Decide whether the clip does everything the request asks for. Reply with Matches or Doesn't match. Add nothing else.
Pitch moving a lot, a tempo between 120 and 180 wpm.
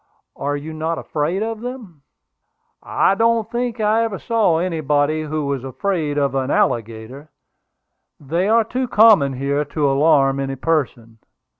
Matches